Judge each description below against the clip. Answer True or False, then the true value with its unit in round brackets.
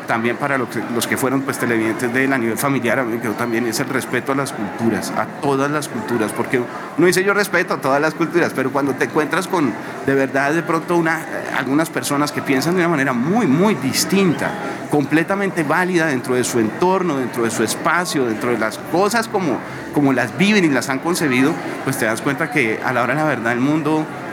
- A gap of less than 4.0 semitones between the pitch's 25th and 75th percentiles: False (4.6 semitones)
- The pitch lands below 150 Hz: True (140 Hz)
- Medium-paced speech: False (220 wpm)